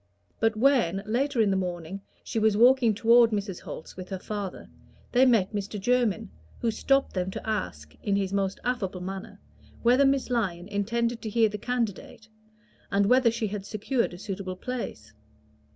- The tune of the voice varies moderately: Yes, average, 3.5 semitones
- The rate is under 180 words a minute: Yes, average, 170 wpm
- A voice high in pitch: Yes, high, 215 Hz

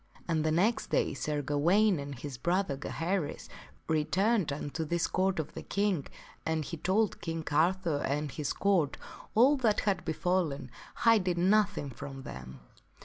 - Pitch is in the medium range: Yes, medium, 165 Hz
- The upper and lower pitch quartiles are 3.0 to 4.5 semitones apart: No, average, 5.0 semitones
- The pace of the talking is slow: No, average, 150 wpm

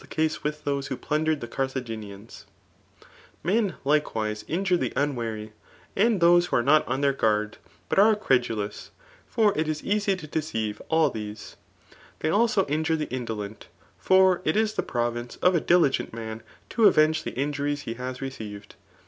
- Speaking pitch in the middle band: Yes, medium, 145 Hz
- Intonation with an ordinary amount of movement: No, wide, 6.7 semitones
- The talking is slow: No, average, 160 wpm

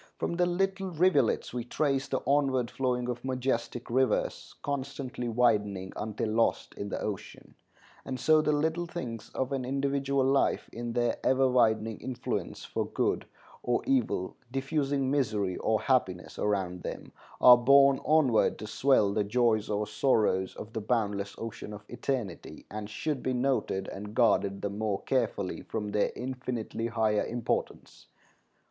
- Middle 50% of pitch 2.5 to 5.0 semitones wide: Yes, average, 4.2 semitones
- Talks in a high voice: No, low, 120 Hz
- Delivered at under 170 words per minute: Yes, average, 150 wpm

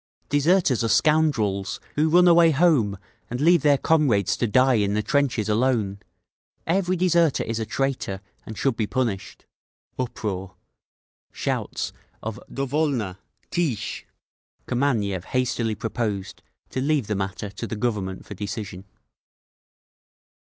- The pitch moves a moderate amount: No, wide, 6.1 semitones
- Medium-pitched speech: No, low, 120 Hz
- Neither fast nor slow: No, slow, 130 wpm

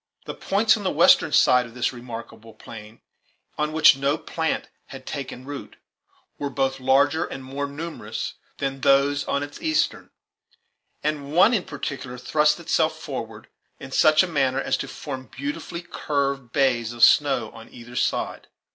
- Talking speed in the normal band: Yes, average, 160 wpm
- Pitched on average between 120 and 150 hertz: Yes, medium, 140 Hz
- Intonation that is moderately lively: Yes, average, 3.0 semitones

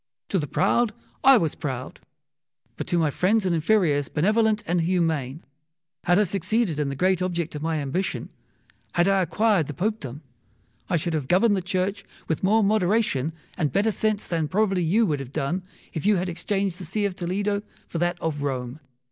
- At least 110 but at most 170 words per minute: No, average, 190 wpm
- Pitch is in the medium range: Yes, medium, 180 Hz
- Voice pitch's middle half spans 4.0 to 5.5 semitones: Yes, average, 4.5 semitones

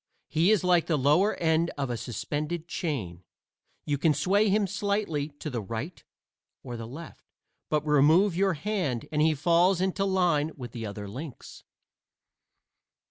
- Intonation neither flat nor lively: Yes, average, 5.0 semitones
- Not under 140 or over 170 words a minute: Yes, average, 155 wpm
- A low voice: No, medium, 155 Hz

